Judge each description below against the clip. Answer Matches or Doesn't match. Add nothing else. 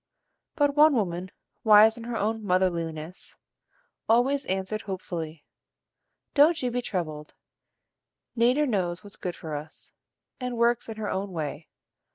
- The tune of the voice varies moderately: Doesn't match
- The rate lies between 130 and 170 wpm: Matches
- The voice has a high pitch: Matches